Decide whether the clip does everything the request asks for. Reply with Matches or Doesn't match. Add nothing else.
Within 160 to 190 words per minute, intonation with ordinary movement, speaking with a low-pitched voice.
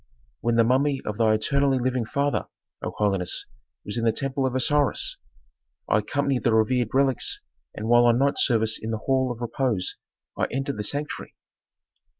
Matches